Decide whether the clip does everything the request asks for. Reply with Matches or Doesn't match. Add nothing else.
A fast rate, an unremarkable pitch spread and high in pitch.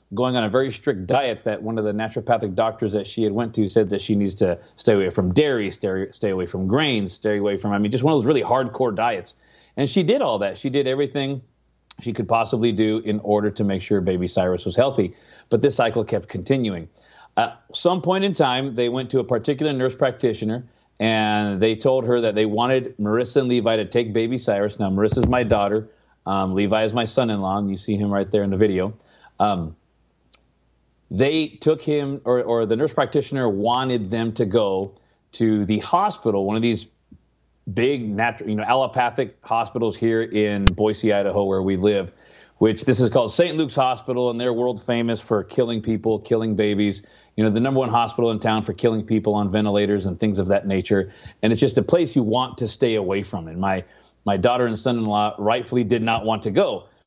Doesn't match